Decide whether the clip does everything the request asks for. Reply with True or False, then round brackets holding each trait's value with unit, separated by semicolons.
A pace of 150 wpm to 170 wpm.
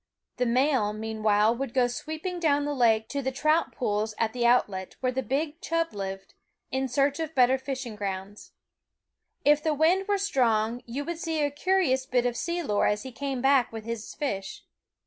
False (195 wpm)